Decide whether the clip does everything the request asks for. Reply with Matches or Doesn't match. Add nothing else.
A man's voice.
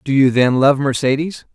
Matches